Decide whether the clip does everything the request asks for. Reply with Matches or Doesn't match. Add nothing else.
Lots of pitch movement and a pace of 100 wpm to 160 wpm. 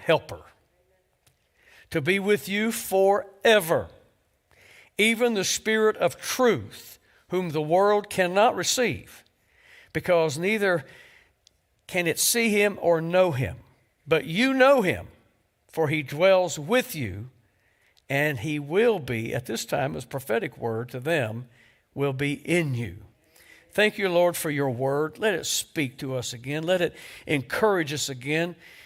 Matches